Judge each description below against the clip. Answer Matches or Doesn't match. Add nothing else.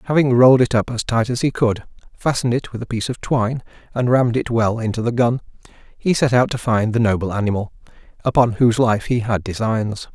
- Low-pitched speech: Matches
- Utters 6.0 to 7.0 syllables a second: Matches